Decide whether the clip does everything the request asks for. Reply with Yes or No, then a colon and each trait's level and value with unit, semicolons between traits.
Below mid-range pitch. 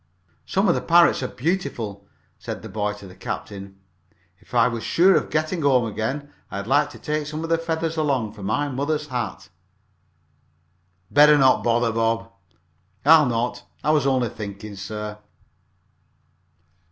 Yes: low, 125 Hz